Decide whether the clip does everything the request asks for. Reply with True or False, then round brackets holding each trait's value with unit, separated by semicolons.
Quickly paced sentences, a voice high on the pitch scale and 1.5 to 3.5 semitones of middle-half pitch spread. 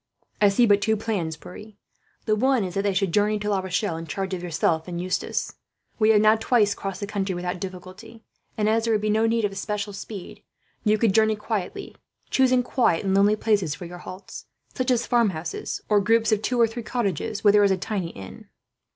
True (220 wpm; 205 Hz; 2.9 semitones)